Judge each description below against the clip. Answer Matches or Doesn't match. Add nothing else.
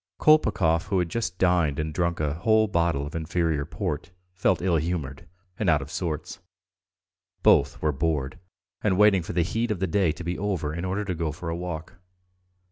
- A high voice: Doesn't match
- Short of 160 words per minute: Doesn't match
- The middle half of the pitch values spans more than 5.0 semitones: Doesn't match